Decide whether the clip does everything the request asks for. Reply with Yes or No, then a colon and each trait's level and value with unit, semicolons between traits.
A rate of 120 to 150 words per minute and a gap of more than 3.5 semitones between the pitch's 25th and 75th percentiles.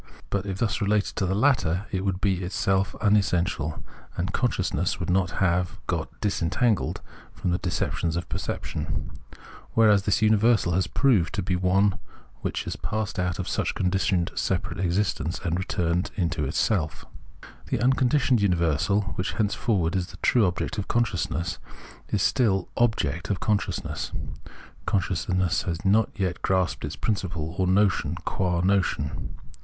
No: average, 145 wpm; average, 2.8 semitones